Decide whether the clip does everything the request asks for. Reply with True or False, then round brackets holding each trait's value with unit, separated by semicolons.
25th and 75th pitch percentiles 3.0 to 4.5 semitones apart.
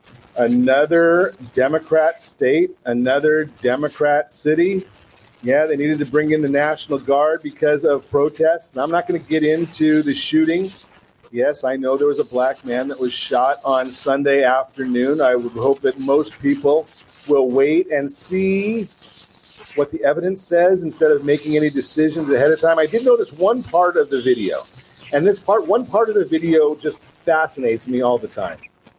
True (4.1 semitones)